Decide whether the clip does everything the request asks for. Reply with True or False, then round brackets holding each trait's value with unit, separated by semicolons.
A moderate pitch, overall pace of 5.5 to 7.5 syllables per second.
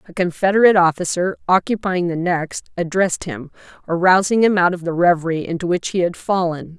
True (180 Hz; 5.6 syllables/s)